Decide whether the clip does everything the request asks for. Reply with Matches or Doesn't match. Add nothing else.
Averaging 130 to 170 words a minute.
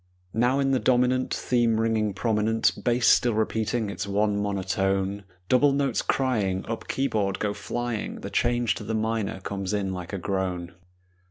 Matches